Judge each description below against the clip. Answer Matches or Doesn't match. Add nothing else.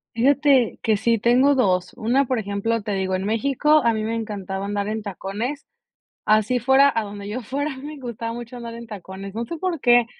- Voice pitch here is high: Matches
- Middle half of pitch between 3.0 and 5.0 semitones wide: Matches